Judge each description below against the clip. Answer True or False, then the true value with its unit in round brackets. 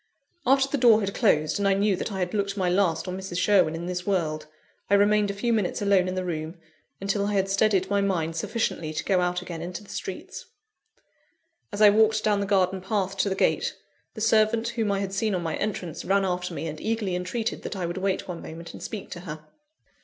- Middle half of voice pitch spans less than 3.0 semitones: True (2.6 semitones)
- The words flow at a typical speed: False (235 wpm)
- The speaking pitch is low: False (195 Hz)